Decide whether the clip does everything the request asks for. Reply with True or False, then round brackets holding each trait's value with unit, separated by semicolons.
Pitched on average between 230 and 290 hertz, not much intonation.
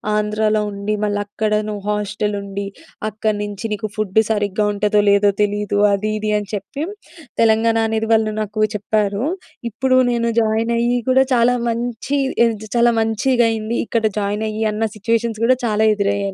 False (215 Hz; 1.7 semitones)